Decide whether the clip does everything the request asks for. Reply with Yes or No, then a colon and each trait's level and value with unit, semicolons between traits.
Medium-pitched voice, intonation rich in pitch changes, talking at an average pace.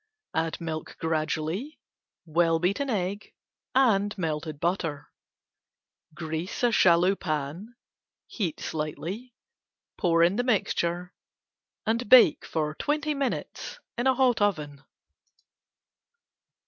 No: medium, 180 Hz; wide, 6.1 semitones; slow, 85 wpm